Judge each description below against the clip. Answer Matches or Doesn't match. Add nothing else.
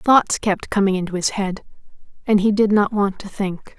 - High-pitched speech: Matches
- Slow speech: Doesn't match